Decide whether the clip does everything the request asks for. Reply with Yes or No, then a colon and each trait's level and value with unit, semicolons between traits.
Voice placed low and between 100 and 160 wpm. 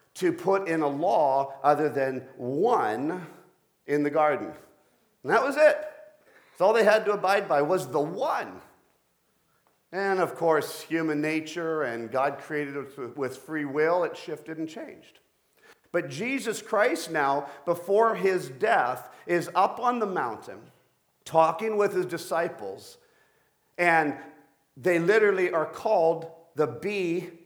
No: medium, 165 Hz; average, 140 wpm